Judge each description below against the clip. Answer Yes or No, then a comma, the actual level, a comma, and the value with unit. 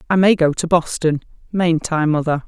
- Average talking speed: Yes, average, 195 wpm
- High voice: No, medium, 165 Hz